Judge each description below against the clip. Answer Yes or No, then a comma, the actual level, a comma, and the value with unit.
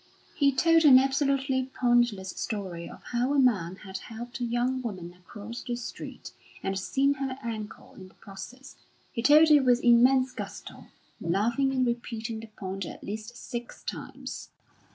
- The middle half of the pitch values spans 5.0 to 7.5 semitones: No, average, 4.1 semitones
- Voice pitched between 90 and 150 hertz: No, high, 240 Hz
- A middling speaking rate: Yes, average, 160 wpm